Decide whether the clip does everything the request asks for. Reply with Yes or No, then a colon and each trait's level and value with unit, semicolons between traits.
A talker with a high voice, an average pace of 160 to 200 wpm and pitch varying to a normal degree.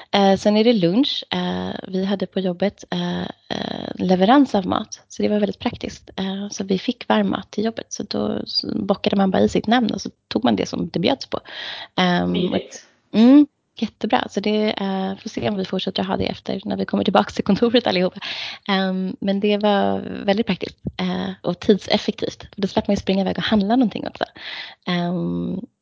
Yes: high, 200 Hz; average, 175 wpm; average, 3.0 semitones